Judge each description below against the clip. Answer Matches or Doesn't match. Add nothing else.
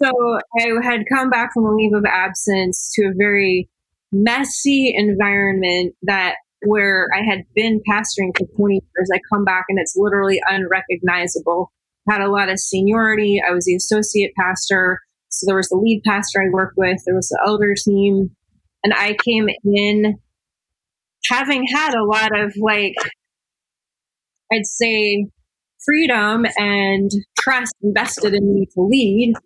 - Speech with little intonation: Matches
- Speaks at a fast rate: Doesn't match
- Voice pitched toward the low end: Doesn't match